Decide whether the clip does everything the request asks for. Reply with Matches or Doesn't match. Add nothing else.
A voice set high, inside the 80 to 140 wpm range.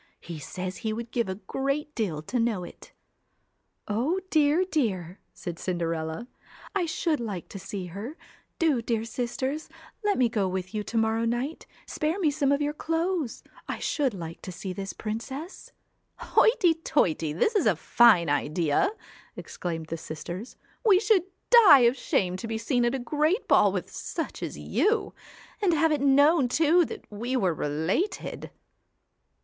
Doesn't match